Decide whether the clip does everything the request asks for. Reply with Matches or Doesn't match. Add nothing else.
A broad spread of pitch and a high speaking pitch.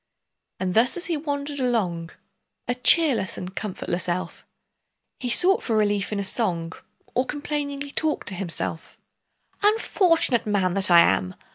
Matches